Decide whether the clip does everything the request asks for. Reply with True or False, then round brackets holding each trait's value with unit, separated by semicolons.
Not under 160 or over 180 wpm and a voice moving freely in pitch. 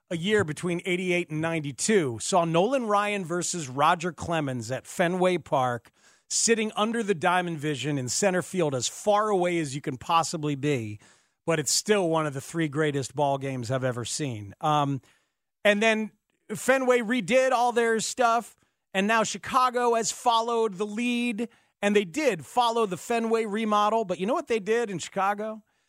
True (170 wpm; 6.5 semitones)